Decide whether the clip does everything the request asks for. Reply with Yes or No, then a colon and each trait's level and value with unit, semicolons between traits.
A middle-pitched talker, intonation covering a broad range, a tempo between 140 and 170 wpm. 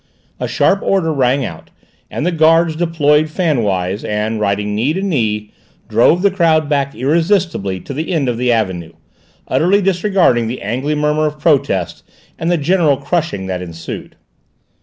Yes: medium, 145 Hz; wide, 7.3 semitones; average, 160 wpm